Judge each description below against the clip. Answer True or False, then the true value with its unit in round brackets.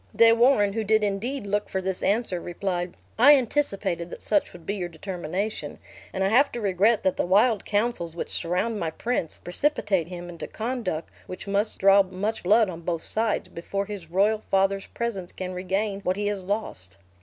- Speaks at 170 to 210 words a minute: True (190 wpm)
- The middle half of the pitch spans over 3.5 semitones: False (3.2 semitones)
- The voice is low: False (195 Hz)